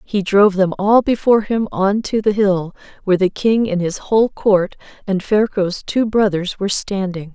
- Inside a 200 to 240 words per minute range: No, average, 190 wpm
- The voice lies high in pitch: Yes, high, 200 Hz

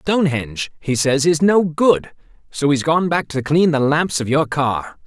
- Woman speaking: No, male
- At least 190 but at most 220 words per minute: Yes, average, 200 wpm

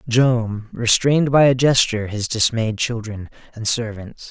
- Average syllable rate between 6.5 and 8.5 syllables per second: No, 4.4 syllables/s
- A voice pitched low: Yes, low, 115 Hz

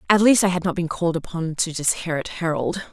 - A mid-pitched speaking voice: Yes, medium, 170 Hz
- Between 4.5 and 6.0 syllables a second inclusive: No, 6.3 syllables/s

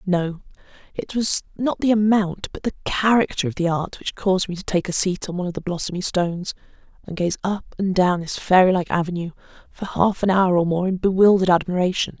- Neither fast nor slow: No, fast, 210 wpm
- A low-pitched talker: No, medium, 185 Hz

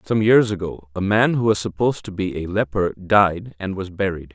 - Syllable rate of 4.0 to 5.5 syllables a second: Yes, 5.1 syllables/s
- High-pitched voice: No, very low, 95 Hz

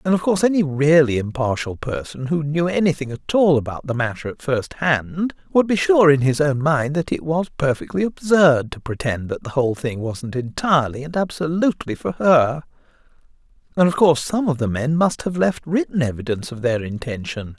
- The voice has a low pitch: No, medium, 150 Hz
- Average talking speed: Yes, average, 195 wpm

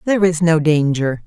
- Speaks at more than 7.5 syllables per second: No, 5.4 syllables/s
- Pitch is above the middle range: No, medium, 165 Hz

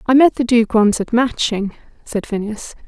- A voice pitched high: Yes, high, 230 Hz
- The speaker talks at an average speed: Yes, average, 190 wpm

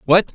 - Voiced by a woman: No, male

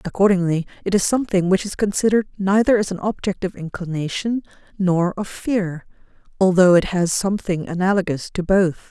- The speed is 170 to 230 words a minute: No, average, 155 wpm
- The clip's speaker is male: No, female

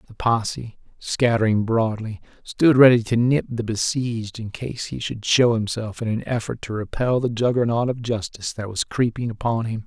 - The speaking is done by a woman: No, male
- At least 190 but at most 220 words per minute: No, average, 180 wpm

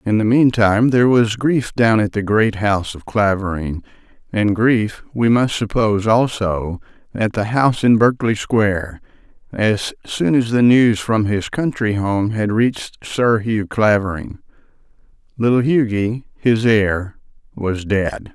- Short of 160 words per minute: Yes, average, 145 wpm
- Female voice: No, male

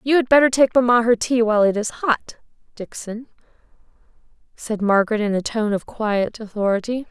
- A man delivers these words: No, female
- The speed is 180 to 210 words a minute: No, average, 170 wpm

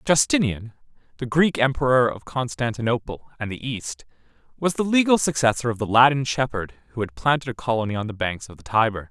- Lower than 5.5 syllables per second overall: No, 5.7 syllables/s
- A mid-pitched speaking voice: No, low, 125 Hz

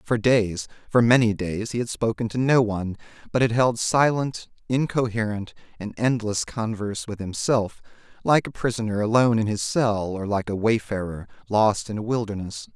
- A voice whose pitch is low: Yes, low, 110 Hz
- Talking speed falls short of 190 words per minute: Yes, average, 170 wpm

